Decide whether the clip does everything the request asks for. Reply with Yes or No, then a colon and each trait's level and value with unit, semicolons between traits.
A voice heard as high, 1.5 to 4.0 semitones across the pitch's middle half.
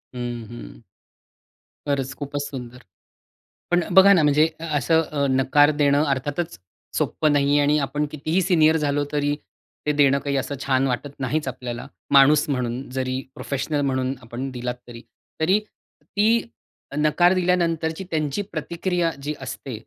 No: medium, 145 Hz; average, 3.2 semitones